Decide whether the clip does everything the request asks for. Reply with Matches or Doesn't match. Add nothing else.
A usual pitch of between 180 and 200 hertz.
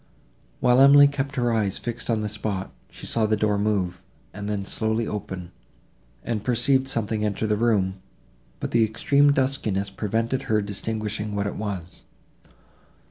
Doesn't match